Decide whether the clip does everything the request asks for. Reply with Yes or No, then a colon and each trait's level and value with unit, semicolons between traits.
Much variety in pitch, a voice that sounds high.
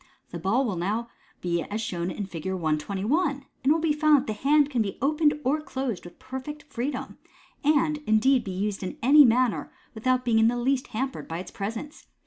Yes: wide, 6.1 semitones; high, 245 Hz